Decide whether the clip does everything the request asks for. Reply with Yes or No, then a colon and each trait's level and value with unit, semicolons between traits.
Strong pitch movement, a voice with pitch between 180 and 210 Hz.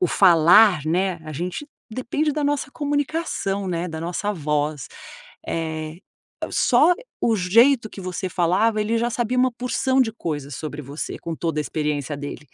Yes: wide, 7.3 semitones; medium, 185 Hz